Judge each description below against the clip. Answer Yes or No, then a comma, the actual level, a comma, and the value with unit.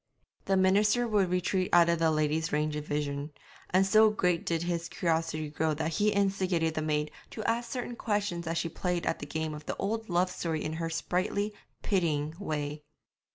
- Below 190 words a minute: No, average, 195 wpm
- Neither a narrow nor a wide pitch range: Yes, average, 3.8 semitones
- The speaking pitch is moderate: Yes, medium, 170 Hz